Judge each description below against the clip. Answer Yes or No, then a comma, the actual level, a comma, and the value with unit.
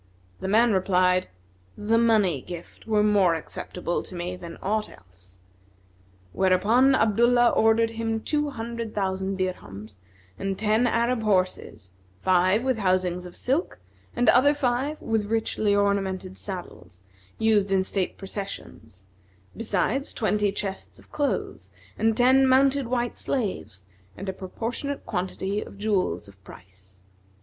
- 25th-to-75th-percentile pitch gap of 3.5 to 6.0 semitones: Yes, average, 4.0 semitones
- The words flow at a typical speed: No, slow, 130 wpm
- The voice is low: No, high, 205 Hz